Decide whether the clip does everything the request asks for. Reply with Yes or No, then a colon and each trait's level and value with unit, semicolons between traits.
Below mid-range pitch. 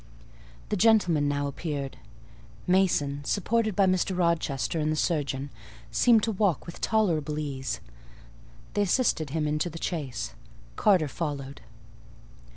No: medium, 160 Hz